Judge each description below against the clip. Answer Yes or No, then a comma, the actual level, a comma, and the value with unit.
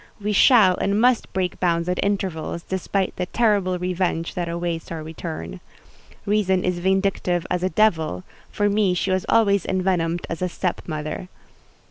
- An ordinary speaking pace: Yes, average, 160 wpm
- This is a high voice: No, medium, 180 Hz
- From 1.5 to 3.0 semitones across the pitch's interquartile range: Yes, average, 2.7 semitones